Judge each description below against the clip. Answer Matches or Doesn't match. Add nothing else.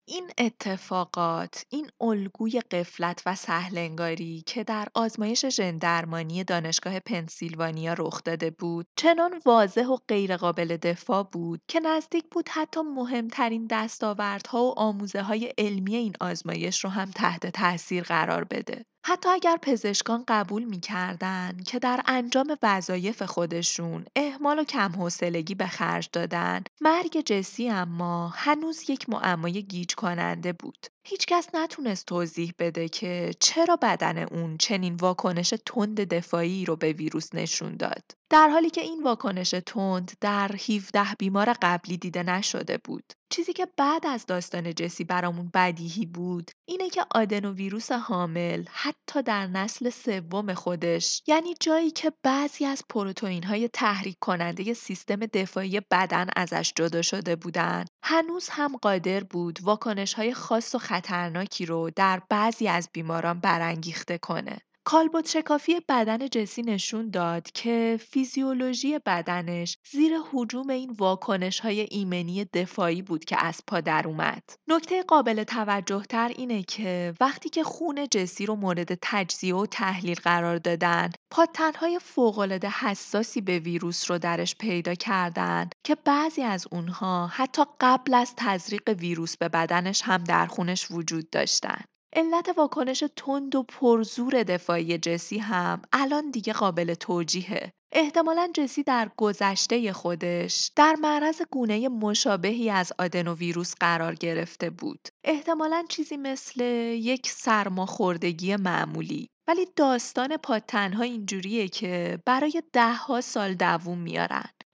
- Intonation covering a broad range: Matches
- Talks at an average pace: Matches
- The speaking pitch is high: Matches